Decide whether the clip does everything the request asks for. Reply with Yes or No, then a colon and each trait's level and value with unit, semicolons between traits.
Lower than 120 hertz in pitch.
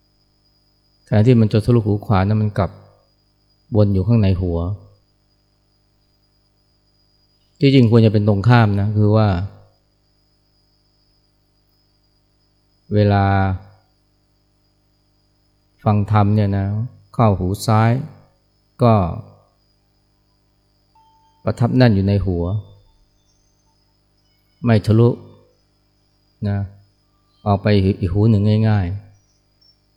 Yes: low, 100 Hz